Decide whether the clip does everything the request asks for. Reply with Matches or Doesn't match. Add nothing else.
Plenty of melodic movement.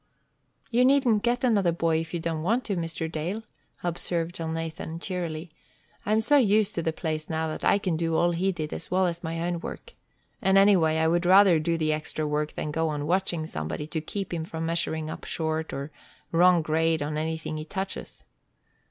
Doesn't match